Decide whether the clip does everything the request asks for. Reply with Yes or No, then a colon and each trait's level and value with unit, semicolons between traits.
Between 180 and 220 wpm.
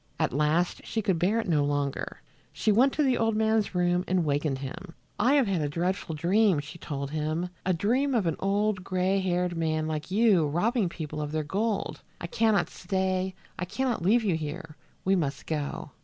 Yes: fast, 205 wpm